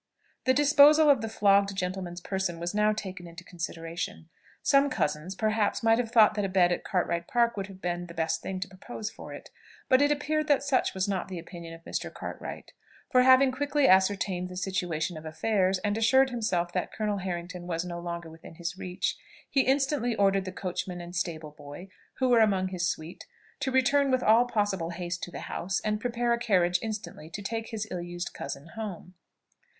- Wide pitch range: No, average, 4.6 semitones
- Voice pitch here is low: No, high, 190 Hz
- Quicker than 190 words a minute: Yes, average, 200 wpm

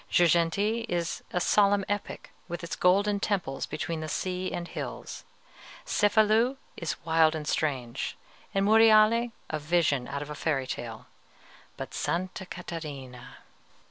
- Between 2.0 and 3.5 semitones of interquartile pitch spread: No, average, 5.0 semitones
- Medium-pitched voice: Yes, medium, 175 Hz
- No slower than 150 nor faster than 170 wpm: No, slow, 135 wpm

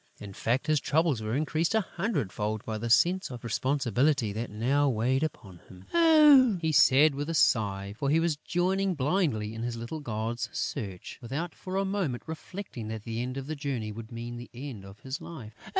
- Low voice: Yes, low, 130 Hz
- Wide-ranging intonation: Yes, wide, 6.2 semitones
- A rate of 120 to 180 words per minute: No, average, 200 wpm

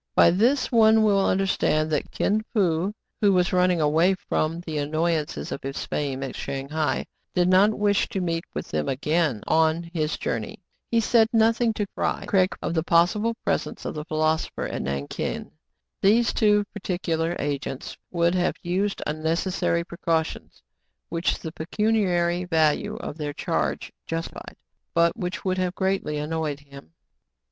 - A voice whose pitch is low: No, medium, 170 Hz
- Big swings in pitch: No, average, 3.9 semitones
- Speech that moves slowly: No, average, 155 wpm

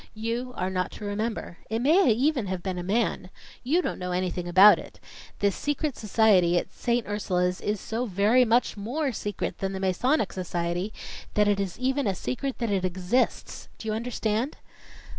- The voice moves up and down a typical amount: Yes, average, 4.7 semitones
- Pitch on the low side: No, high, 210 Hz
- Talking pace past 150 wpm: Yes, average, 180 wpm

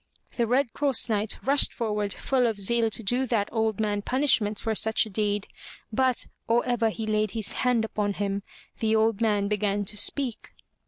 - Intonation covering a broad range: No, narrow, 2.4 semitones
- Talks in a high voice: Yes, high, 220 Hz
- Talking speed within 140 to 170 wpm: No, average, 190 wpm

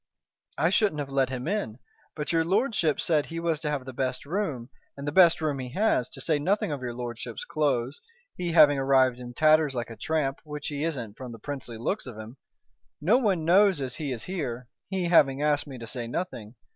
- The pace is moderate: No, fast, 220 wpm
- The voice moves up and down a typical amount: Yes, average, 4.7 semitones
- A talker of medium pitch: Yes, medium, 145 Hz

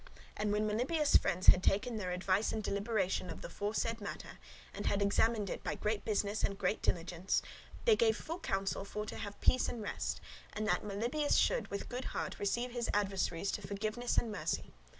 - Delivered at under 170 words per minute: No, average, 190 wpm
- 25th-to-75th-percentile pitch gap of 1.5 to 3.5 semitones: Yes, average, 2.8 semitones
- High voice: Yes, high, 210 Hz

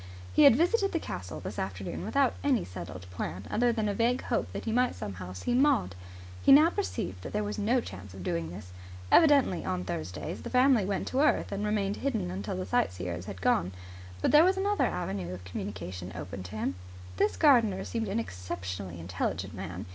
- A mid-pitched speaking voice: Yes, medium, 155 Hz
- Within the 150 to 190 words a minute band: No, average, 200 wpm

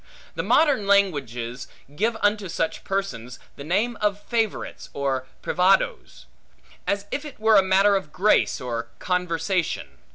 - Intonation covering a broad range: Yes, wide, 6.7 semitones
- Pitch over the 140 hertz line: Yes, high, 190 Hz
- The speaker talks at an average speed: No, slow, 130 wpm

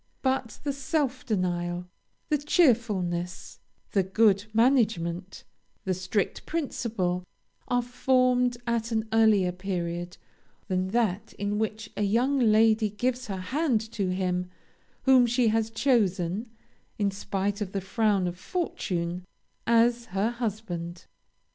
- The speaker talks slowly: Yes, slow, 125 wpm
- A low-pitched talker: No, high, 215 Hz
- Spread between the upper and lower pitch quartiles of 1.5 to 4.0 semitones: No, average, 4.6 semitones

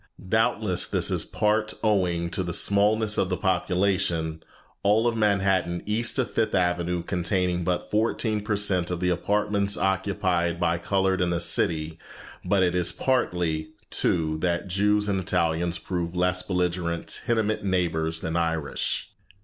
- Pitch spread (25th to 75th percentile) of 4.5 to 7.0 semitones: No, average, 3.0 semitones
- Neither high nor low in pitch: No, very low, 90 Hz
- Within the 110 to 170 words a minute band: Yes, average, 150 wpm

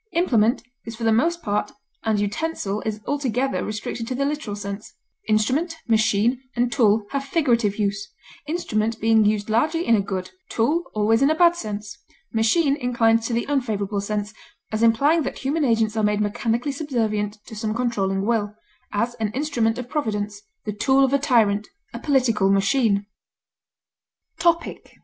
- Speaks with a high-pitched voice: Yes, high, 225 Hz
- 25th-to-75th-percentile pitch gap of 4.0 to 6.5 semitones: Yes, average, 4.5 semitones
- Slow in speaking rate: No, average, 165 wpm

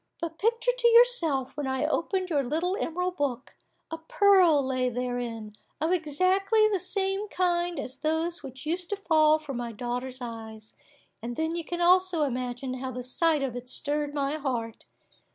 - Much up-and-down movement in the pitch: Yes, wide, 5.9 semitones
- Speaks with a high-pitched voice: Yes, very high, 305 Hz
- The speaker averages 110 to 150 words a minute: No, average, 170 wpm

